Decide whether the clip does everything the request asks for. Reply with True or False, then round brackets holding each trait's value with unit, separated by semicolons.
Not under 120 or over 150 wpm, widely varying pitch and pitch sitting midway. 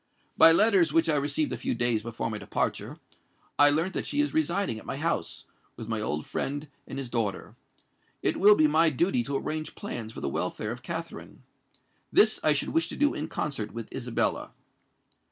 False (195 wpm; 6.0 semitones; 145 Hz)